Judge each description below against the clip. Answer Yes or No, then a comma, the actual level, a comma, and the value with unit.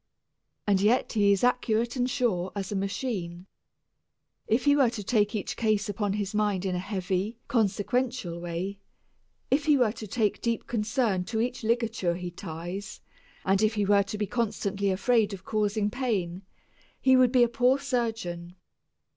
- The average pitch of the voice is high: Yes, high, 210 Hz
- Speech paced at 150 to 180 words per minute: Yes, average, 170 wpm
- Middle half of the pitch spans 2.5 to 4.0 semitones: Yes, average, 3.7 semitones